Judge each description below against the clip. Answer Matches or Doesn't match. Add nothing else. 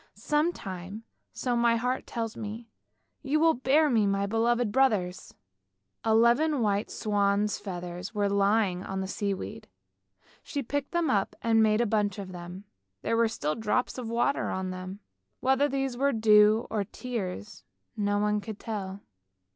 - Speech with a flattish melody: Doesn't match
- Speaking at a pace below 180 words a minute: Matches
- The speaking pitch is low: Doesn't match